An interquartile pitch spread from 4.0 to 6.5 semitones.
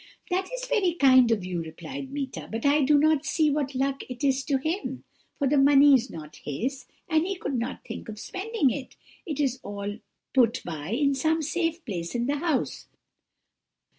Yes: average, 4.4 semitones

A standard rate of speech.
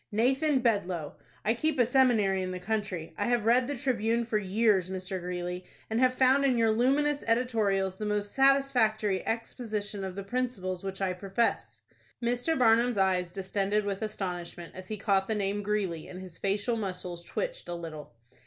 Yes: average, 175 wpm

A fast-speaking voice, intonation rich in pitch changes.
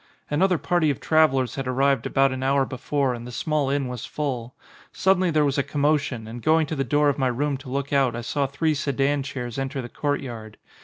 No: fast, 225 wpm; narrow, 2.5 semitones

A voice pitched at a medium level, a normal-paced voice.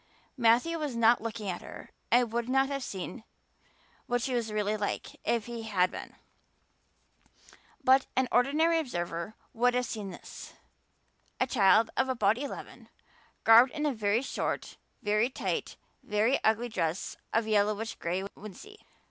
No: high, 230 Hz; average, 150 wpm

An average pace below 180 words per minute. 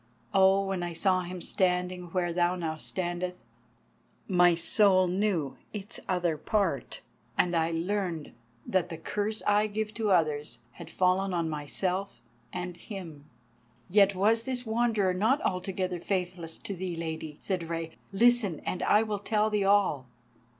Yes: average, 150 wpm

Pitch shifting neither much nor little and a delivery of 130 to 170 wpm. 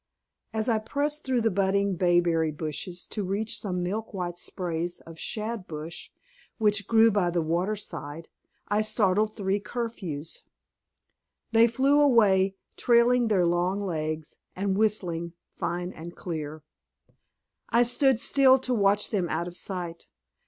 Yes: average, 4.3 semitones; average, 140 wpm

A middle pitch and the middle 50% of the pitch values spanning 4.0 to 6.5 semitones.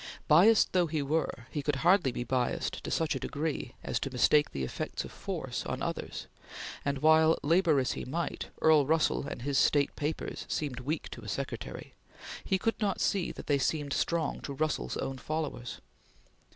No: medium, 150 Hz; average, 3.2 semitones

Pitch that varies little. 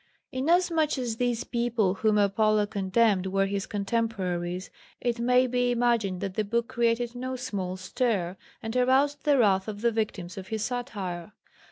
No: average, 4.0 semitones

